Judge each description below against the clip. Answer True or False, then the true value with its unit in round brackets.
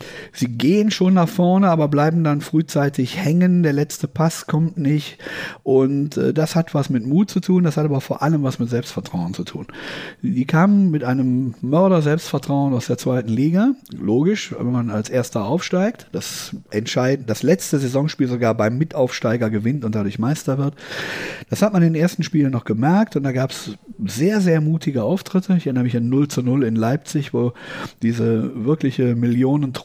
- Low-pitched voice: False (145 Hz)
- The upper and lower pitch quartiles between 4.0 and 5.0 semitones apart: True (4.7 semitones)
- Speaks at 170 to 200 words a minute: True (180 wpm)